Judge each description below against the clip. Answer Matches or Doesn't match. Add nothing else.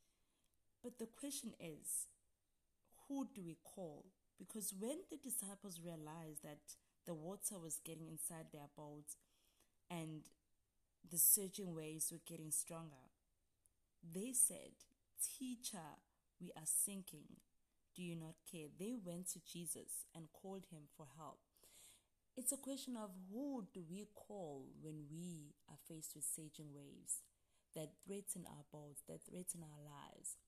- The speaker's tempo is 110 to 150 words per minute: Matches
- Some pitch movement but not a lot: Matches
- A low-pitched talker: Doesn't match